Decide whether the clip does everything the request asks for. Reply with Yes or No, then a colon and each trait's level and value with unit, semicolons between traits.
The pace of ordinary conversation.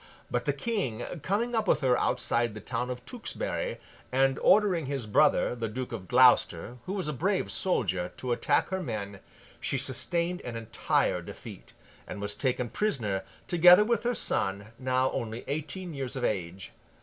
Yes: average, 170 wpm